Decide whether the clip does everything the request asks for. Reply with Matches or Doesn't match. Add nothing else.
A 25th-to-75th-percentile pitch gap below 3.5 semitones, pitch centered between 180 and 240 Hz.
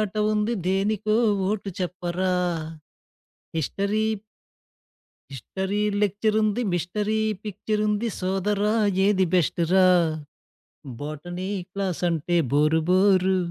Matches